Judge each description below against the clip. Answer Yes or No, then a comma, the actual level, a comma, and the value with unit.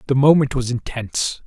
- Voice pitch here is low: Yes, low, 130 Hz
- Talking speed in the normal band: Yes, average, 165 wpm